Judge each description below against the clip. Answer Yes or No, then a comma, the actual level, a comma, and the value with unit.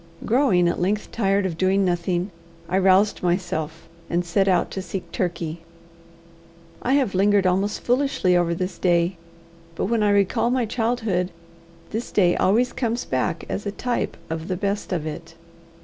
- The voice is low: No, high, 190 Hz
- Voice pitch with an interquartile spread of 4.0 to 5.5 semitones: No, average, 3.2 semitones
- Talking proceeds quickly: No, average, 165 wpm